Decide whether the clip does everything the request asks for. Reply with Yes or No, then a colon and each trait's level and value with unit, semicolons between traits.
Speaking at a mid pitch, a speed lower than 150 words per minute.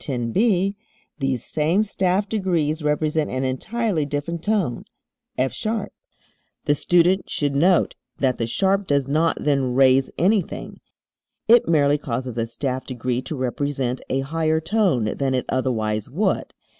Yes: medium, 145 Hz; average, 140 wpm